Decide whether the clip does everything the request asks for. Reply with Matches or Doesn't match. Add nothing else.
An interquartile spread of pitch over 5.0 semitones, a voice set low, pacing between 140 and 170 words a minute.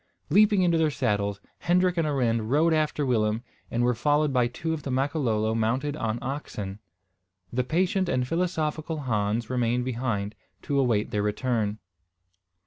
Matches